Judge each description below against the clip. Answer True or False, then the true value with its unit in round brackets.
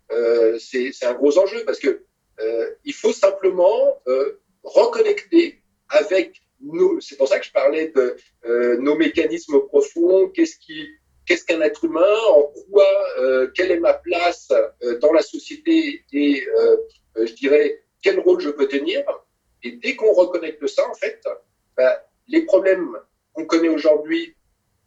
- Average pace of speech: True (160 wpm)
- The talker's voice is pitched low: False (295 Hz)